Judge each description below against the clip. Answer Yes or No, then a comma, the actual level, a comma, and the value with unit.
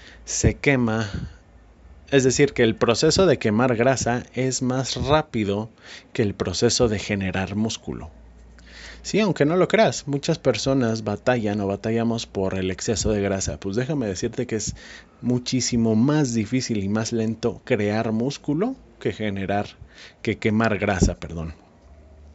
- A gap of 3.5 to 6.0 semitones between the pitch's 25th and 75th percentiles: Yes, average, 4.6 semitones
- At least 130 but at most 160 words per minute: Yes, average, 140 wpm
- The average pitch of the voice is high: No, low, 110 Hz